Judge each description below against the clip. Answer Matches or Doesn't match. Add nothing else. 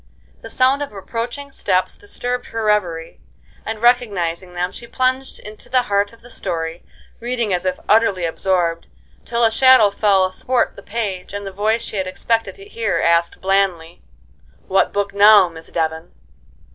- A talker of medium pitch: Doesn't match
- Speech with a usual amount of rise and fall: Matches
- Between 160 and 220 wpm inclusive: Matches